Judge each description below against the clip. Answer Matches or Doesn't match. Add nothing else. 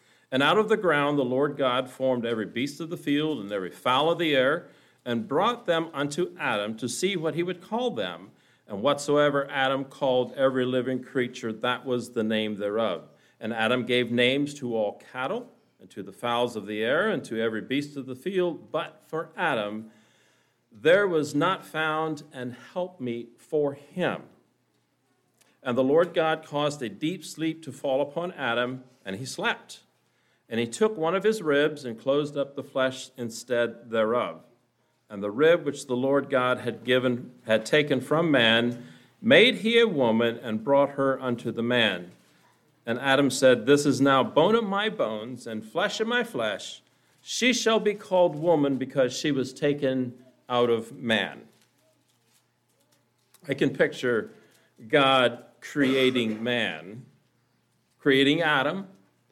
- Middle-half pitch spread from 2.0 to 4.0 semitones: Doesn't match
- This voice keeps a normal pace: Matches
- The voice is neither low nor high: Doesn't match